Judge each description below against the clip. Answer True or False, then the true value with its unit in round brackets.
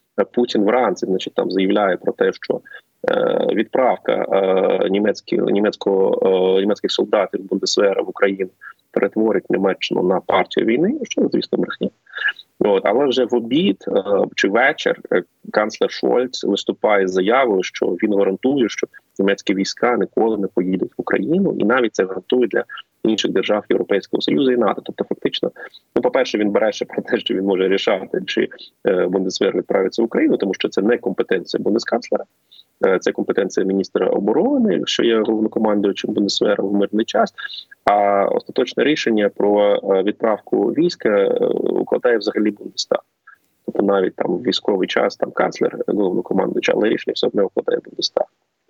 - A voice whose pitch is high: True (375 Hz)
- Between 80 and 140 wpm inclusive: False (150 wpm)